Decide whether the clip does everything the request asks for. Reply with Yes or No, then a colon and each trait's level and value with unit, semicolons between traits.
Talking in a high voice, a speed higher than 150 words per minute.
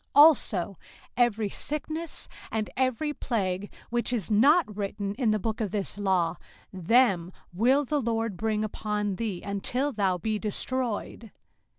No: high, 215 Hz; average, 145 wpm